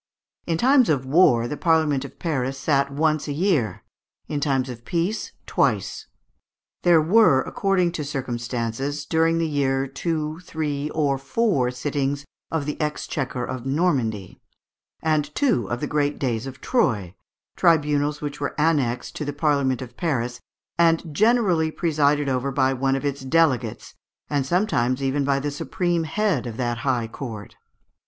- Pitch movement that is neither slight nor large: Yes, average, 3.6 semitones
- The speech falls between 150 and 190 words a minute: Yes, average, 155 wpm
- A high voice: No, medium, 145 Hz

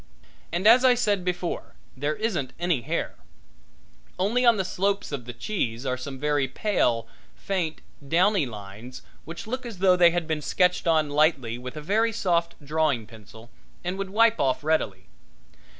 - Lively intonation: Yes, wide, 7.0 semitones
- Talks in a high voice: No, medium, 165 Hz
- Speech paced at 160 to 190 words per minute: Yes, average, 165 wpm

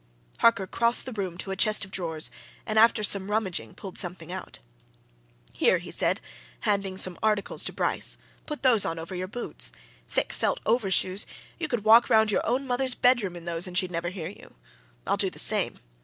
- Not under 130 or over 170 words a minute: No, average, 195 wpm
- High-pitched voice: Yes, high, 200 Hz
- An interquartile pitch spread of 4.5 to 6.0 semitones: No, average, 4.1 semitones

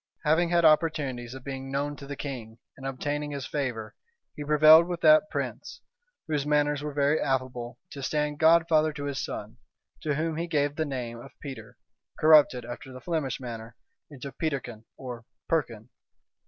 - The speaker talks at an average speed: Yes, average, 170 wpm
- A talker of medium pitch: Yes, medium, 145 Hz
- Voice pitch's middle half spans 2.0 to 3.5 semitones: Yes, average, 3.0 semitones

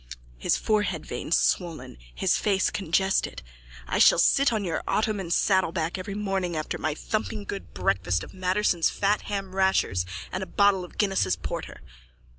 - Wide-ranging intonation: No, average, 3.8 semitones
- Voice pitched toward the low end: No, high, 190 Hz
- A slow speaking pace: No, average, 150 wpm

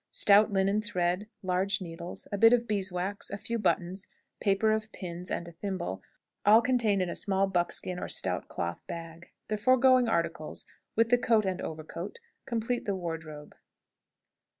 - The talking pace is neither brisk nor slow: Yes, average, 160 wpm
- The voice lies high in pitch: Yes, high, 195 Hz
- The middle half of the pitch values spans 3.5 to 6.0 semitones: Yes, average, 3.8 semitones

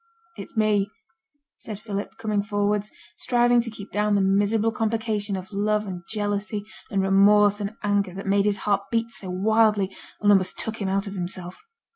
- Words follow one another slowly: No, average, 175 wpm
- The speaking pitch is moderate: No, high, 205 Hz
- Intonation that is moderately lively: No, narrow, 1.5 semitones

